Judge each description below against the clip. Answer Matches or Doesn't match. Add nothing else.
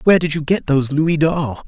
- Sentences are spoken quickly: Matches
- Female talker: Doesn't match